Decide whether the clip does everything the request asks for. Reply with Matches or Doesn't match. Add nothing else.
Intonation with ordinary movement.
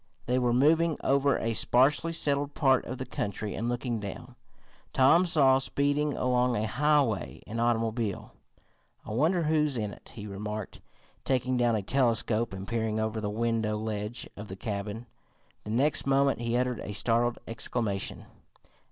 Matches